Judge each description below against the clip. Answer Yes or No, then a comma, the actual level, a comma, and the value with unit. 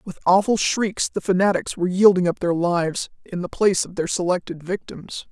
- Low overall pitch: No, medium, 185 Hz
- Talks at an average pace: Yes, average, 190 wpm